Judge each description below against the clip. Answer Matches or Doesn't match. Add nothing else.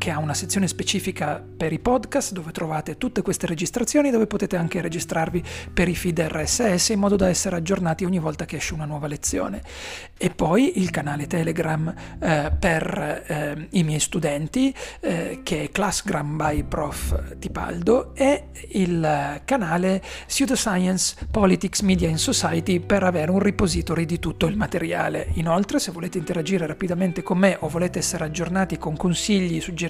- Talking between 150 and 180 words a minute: Matches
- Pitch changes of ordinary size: Matches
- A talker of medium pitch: Matches